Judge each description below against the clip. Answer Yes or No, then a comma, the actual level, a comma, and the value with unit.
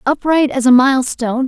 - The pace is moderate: Yes, average, 165 wpm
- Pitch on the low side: No, very high, 265 Hz